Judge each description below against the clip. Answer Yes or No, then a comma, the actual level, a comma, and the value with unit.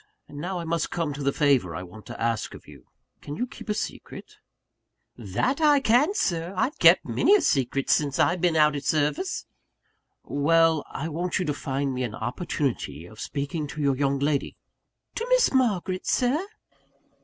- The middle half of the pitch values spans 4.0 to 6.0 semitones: Yes, average, 5.1 semitones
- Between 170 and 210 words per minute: Yes, average, 190 wpm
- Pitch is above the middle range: No, medium, 150 Hz